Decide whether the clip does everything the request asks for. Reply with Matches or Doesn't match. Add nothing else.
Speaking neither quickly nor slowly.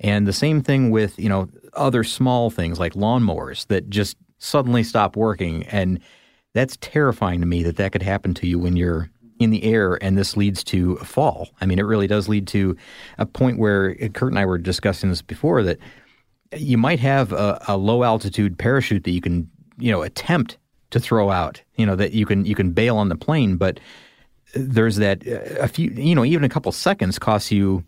Doesn't match